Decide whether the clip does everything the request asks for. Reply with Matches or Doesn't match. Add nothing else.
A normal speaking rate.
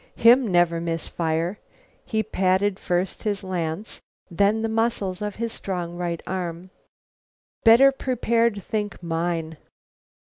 Doesn't match